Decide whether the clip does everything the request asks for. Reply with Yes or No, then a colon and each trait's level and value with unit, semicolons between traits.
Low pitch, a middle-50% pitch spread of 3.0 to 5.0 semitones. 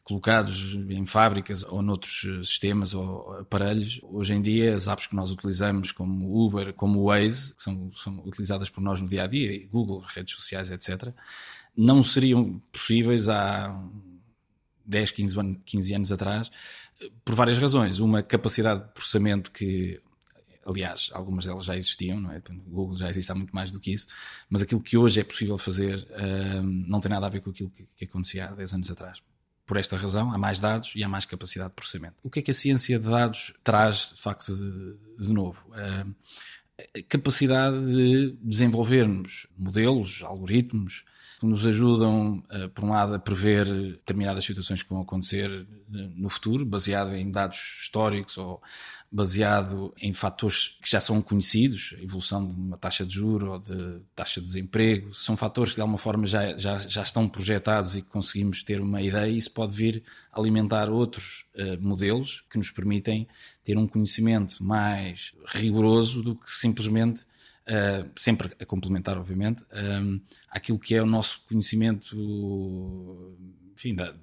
No: low, 100 Hz; narrow, 2.4 semitones